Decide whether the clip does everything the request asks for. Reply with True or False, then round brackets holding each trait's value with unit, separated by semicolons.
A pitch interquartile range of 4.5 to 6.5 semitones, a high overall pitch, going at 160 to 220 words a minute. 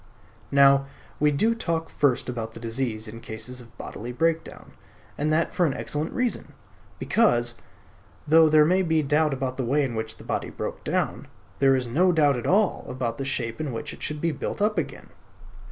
False (5.1 semitones; 140 Hz; 195 wpm)